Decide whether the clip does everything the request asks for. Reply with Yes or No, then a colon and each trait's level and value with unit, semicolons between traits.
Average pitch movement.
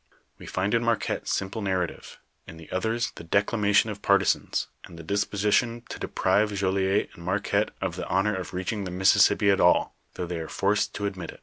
No: narrow, 2.2 semitones